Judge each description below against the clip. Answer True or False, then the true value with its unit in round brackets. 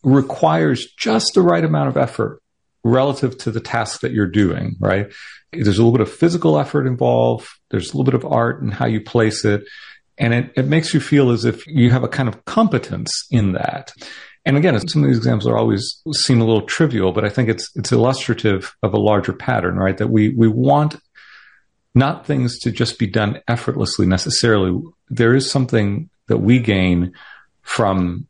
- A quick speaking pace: False (195 wpm)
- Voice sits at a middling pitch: False (115 Hz)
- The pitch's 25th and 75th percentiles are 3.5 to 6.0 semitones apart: True (4.0 semitones)